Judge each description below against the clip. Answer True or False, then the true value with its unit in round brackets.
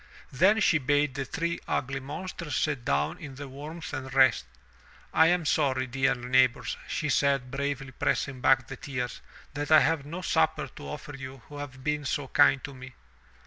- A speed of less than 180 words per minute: False (185 wpm)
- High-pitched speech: False (135 Hz)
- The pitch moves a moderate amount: False (2.3 semitones)